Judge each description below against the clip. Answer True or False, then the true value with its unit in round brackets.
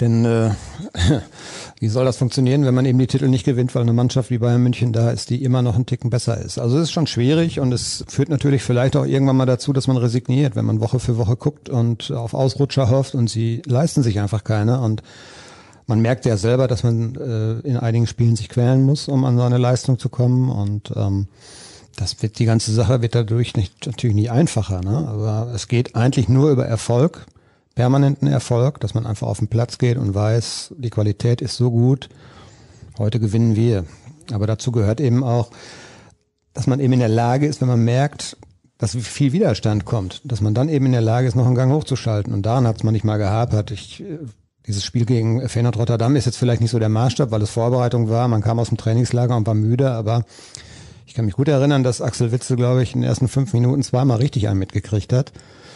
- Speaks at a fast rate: True (225 wpm)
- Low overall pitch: True (120 Hz)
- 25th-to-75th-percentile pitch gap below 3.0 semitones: True (2.4 semitones)